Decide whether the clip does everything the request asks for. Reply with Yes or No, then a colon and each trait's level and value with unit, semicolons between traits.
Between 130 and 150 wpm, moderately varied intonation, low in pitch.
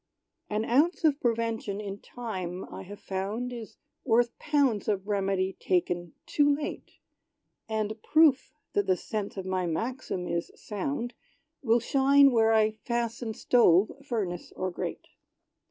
No: average, 140 wpm; average, 4.2 semitones; high, 220 Hz